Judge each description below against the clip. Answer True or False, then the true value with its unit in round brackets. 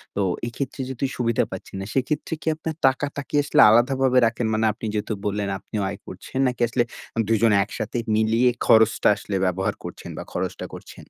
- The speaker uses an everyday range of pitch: True (3.5 semitones)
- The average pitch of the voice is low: True (115 Hz)